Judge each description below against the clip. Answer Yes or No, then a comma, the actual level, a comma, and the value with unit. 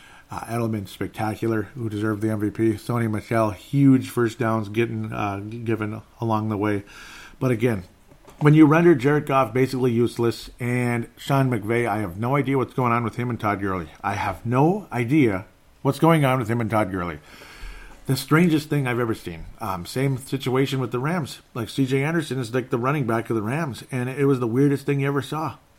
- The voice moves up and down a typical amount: Yes, average, 3.8 semitones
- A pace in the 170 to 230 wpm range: Yes, average, 200 wpm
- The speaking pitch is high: No, low, 120 Hz